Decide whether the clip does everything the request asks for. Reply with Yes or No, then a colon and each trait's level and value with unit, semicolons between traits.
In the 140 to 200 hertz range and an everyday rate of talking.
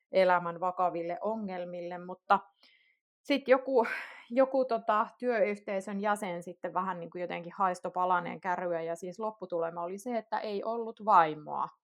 Yes: medium, 185 Hz; average, 130 wpm